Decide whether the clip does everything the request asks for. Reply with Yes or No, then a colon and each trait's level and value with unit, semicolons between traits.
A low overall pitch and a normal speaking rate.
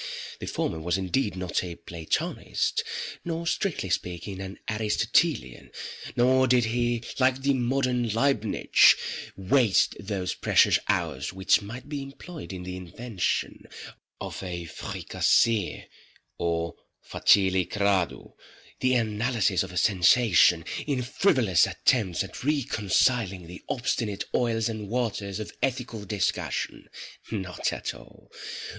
No: low, 105 Hz; slow, 115 wpm